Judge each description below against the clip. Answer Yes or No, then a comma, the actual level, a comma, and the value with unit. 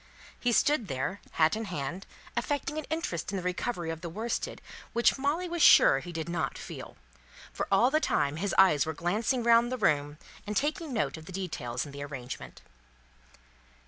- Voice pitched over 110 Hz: Yes, high, 190 Hz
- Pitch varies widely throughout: Yes, wide, 7.5 semitones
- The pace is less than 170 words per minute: No, average, 185 wpm